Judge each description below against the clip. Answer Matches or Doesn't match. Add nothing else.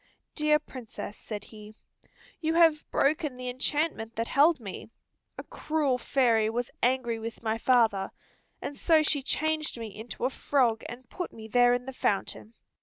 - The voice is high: Matches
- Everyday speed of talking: Matches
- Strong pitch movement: Doesn't match